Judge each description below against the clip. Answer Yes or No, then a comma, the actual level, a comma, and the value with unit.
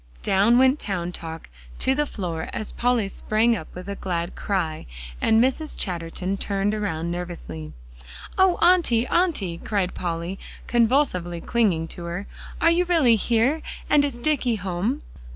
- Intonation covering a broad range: Yes, wide, 6.4 semitones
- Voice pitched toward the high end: Yes, high, 205 Hz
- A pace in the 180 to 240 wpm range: No, average, 150 wpm